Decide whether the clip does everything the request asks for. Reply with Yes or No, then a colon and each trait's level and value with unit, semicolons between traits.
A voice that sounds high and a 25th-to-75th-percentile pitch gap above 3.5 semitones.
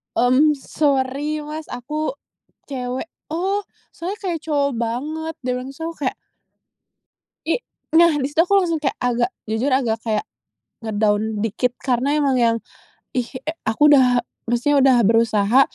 Yes: very high, 270 Hz; average, 4.2 semitones